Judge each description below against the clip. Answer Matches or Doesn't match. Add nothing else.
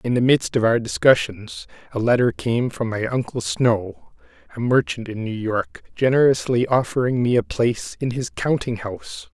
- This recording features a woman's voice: Doesn't match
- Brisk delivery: Doesn't match